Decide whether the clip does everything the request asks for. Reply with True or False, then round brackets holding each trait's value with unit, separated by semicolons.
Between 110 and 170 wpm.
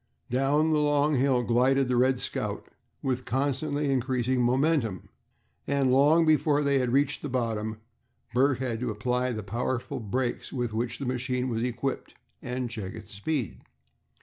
True (150 wpm)